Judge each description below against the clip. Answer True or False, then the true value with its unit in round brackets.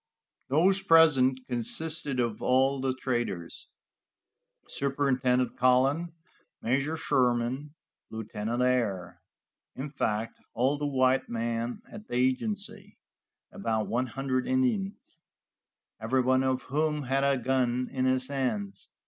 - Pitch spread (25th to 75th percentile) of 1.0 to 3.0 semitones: True (2.7 semitones)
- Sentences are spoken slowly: True (115 wpm)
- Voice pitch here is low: True (130 Hz)